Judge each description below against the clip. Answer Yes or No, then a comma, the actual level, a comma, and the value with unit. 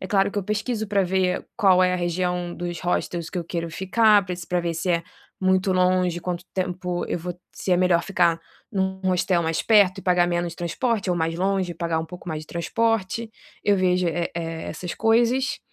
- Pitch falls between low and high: Yes, medium, 180 Hz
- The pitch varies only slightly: Yes, narrow, 1.9 semitones